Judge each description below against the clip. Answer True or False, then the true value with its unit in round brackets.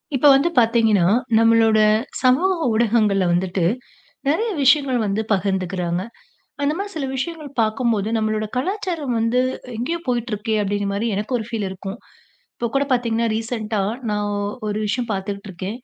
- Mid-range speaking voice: False (225 Hz)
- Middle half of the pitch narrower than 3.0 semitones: False (3.8 semitones)